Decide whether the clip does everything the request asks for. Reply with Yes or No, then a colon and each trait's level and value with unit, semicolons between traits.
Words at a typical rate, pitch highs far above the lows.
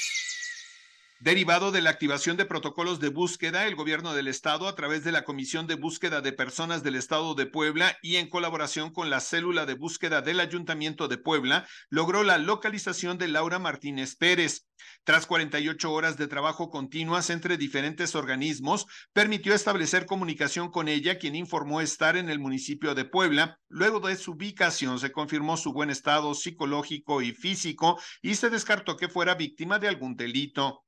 No: average, 170 wpm; average, 3.2 semitones